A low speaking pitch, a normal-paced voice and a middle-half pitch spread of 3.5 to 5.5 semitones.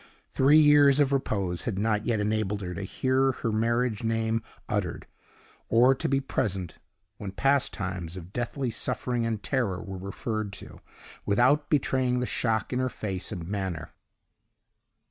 Yes: low, 115 Hz; average, 155 wpm; average, 4.7 semitones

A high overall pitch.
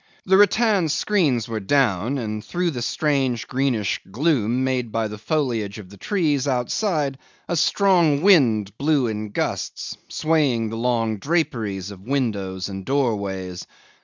No: low, 125 Hz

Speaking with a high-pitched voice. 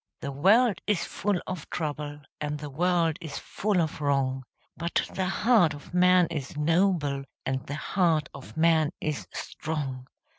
No: medium, 160 Hz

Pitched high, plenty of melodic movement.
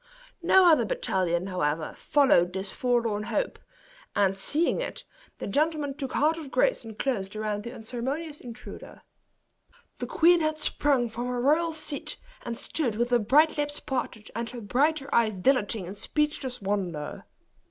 Yes: high, 245 Hz; wide, 6.4 semitones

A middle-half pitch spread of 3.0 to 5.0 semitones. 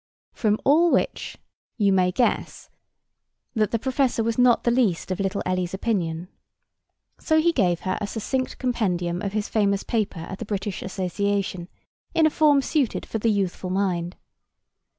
Yes: average, 4.4 semitones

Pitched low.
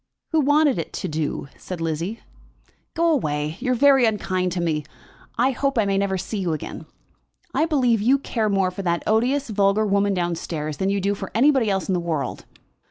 No: high, 200 Hz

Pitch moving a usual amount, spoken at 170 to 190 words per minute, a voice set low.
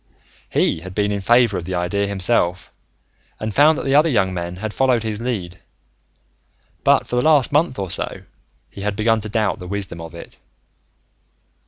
Yes: average, 4.6 semitones; average, 185 wpm; low, 105 Hz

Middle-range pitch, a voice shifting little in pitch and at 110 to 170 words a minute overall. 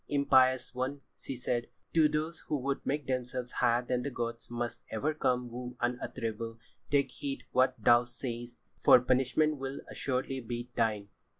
No: low, 125 Hz; narrow, 2.2 semitones; average, 160 wpm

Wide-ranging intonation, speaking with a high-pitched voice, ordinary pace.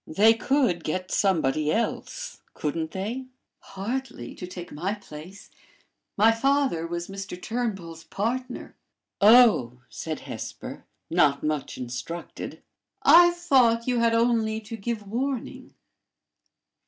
No: wide, 6.2 semitones; high, 205 Hz; slow, 115 wpm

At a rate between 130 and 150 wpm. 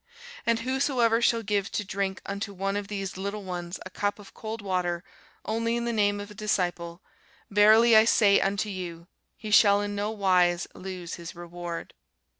No: average, 180 wpm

